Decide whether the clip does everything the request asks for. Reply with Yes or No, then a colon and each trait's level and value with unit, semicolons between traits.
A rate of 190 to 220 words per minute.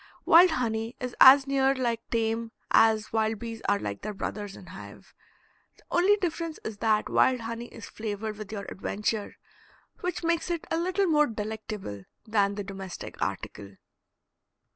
No: average, 160 wpm